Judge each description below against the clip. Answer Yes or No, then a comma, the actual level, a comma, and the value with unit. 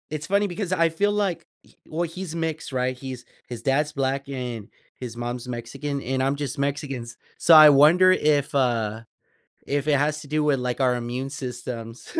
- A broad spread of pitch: No, average, 3.6 semitones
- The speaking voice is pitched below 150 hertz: Yes, medium, 140 Hz